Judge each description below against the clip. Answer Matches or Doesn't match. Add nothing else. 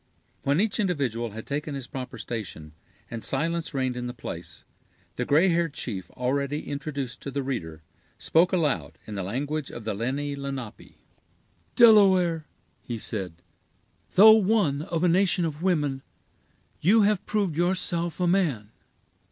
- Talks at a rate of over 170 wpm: Doesn't match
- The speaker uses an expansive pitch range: Matches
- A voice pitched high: Doesn't match